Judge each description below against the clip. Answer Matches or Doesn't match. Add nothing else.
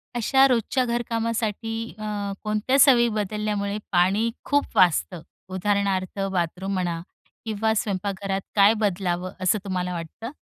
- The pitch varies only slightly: Doesn't match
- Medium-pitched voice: Doesn't match